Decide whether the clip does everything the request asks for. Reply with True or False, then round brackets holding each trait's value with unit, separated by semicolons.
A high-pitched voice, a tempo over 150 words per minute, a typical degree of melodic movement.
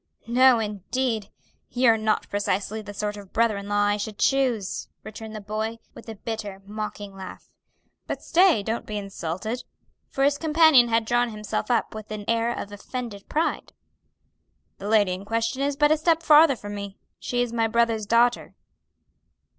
True (220 Hz; 170 wpm; 3.0 semitones)